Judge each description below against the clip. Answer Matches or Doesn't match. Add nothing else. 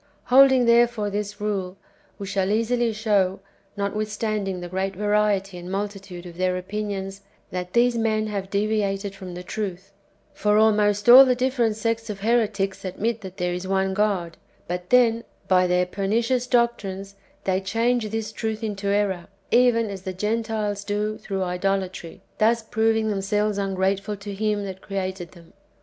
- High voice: Matches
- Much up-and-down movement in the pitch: Doesn't match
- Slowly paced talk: Doesn't match